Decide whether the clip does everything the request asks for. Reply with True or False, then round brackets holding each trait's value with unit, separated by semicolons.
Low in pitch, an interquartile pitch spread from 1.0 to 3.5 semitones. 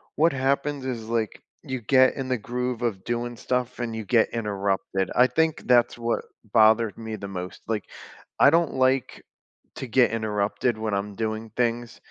True (115 Hz; 2.8 semitones)